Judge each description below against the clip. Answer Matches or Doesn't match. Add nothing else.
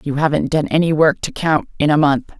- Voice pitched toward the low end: Doesn't match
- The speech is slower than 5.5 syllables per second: Doesn't match